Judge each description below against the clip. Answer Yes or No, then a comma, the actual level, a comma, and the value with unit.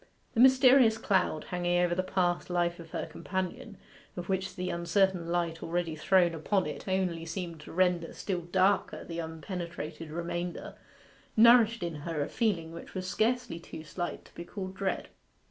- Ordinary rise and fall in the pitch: No, narrow, 2.2 semitones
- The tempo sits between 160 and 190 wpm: Yes, average, 165 wpm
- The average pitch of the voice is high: No, medium, 175 Hz